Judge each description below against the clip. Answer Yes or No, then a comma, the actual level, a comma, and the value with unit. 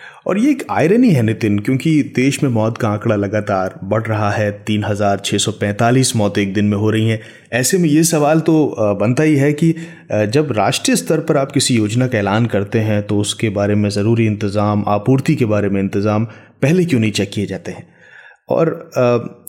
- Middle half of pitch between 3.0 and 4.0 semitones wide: No, average, 4.8 semitones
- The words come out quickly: Yes, fast, 195 wpm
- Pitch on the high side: No, low, 110 Hz